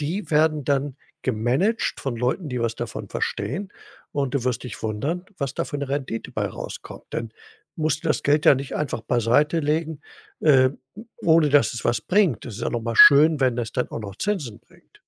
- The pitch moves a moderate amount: Yes, average, 4.4 semitones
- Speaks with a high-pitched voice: No, medium, 140 Hz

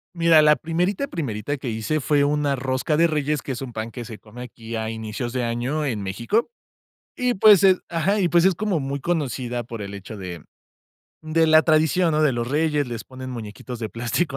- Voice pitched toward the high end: No, medium, 140 Hz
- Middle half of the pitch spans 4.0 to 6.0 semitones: Yes, wide, 5.5 semitones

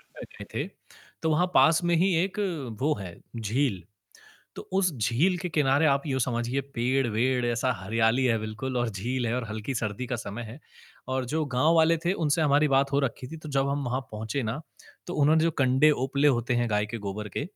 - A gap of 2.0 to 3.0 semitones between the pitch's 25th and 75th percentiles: No, average, 4.4 semitones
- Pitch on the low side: Yes, low, 130 Hz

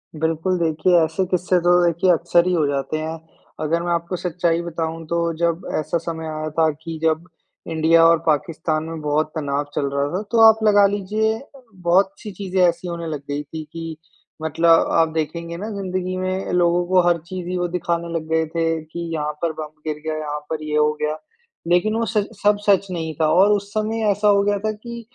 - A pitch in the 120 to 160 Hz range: No, medium, 170 Hz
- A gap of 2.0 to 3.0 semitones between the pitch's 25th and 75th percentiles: Yes, average, 2.7 semitones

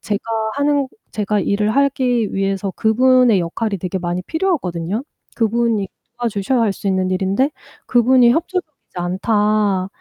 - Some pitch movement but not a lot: Yes, average, 4.6 semitones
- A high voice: Yes, high, 215 Hz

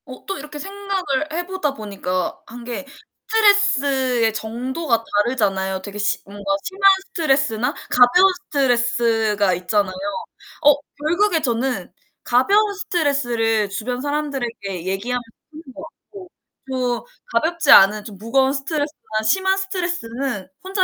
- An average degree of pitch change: No, wide, 6.8 semitones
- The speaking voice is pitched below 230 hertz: No, very high, 260 Hz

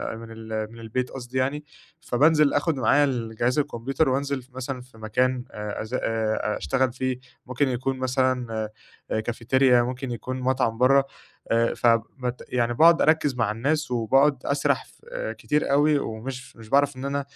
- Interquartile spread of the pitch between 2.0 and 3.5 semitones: Yes, average, 2.9 semitones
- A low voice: Yes, low, 130 Hz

